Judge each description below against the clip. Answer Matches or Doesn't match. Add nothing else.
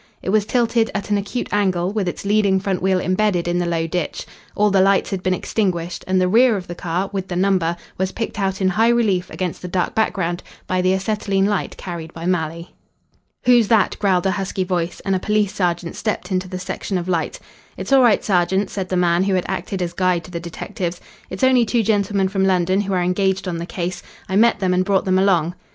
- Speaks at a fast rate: Matches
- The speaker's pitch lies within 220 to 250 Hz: Doesn't match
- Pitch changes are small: Matches